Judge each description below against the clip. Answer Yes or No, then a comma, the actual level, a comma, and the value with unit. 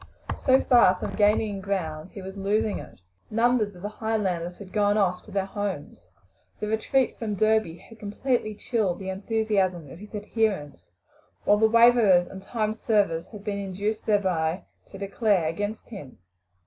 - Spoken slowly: No, average, 160 wpm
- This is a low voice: No, high, 205 Hz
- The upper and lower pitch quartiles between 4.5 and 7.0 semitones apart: No, average, 2.8 semitones